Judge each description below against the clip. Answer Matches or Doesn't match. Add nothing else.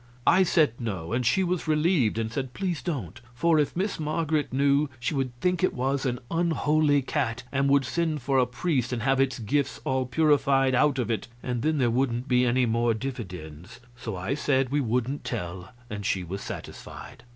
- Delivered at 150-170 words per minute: Doesn't match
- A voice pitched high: Doesn't match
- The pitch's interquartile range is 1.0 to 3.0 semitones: Doesn't match